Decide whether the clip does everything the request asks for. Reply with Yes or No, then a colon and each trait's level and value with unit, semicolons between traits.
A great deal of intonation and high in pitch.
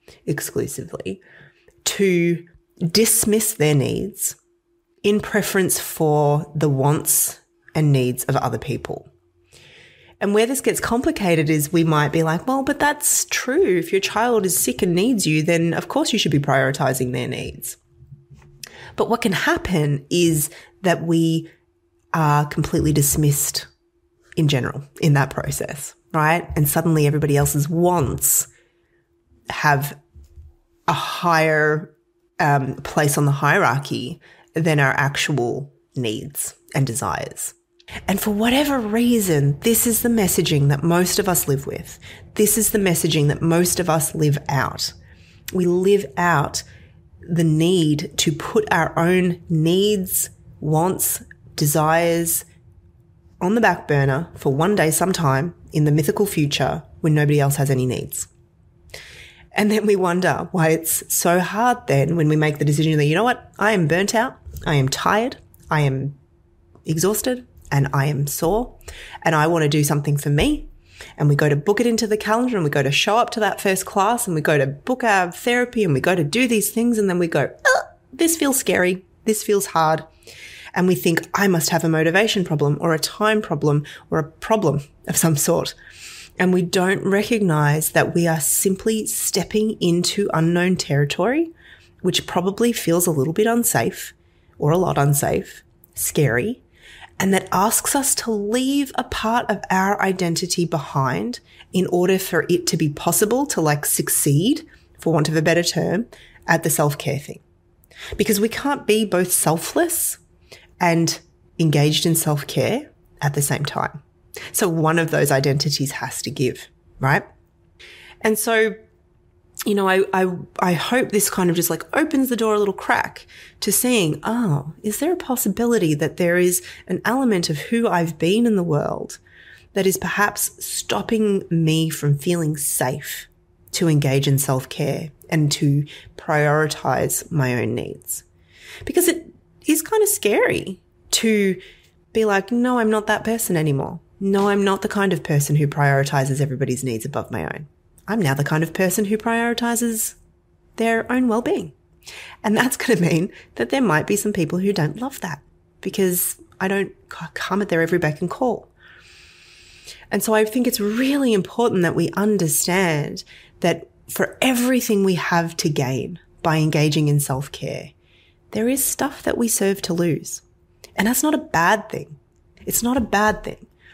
No: wide, 6.1 semitones; medium, 170 Hz